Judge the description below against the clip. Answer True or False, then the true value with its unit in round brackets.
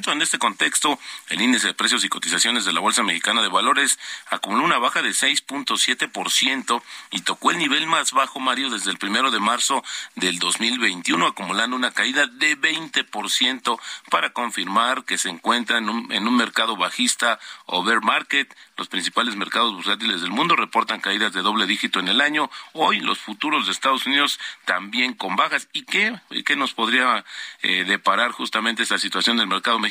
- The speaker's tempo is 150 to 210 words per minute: True (175 wpm)